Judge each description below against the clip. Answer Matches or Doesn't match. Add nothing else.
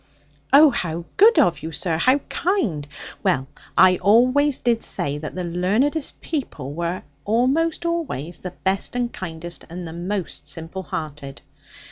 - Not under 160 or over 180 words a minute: Doesn't match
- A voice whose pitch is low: Doesn't match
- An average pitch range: Doesn't match